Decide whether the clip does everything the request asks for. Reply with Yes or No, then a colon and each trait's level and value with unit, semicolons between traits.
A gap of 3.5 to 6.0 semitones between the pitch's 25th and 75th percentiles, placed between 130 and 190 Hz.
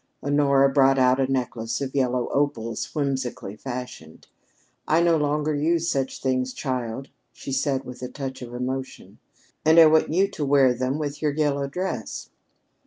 No: narrow, 2.5 semitones; low, 135 Hz